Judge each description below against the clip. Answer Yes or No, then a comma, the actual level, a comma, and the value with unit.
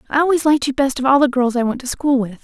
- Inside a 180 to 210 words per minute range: No, fast, 345 wpm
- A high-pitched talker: Yes, very high, 265 Hz